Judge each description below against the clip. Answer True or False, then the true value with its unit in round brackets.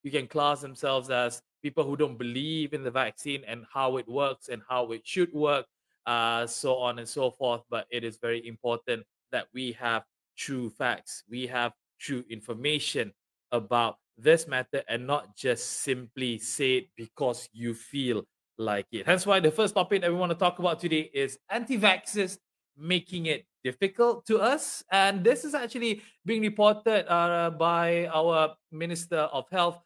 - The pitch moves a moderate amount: False (6.2 semitones)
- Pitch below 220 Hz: True (140 Hz)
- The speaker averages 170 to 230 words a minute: True (175 wpm)